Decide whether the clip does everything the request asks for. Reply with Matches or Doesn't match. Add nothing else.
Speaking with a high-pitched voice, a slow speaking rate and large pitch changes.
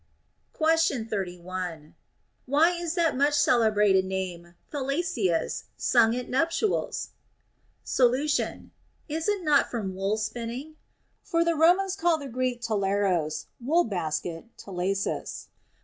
Matches